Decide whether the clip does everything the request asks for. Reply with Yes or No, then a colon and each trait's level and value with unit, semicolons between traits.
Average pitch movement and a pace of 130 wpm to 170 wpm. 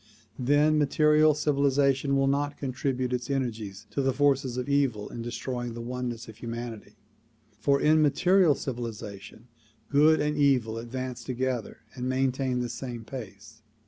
Yes: average, 3.0 semitones; average, 145 wpm